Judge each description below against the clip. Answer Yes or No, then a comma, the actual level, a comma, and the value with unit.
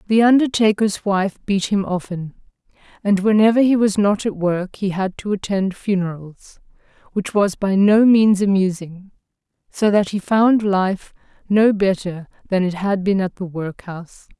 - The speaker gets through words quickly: No, average, 160 wpm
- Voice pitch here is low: No, high, 195 Hz